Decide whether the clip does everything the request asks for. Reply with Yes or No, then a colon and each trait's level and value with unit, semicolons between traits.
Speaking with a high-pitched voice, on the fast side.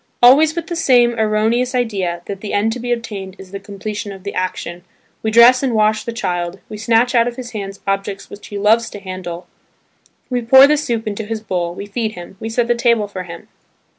Yes: high, 215 Hz; fast, 225 wpm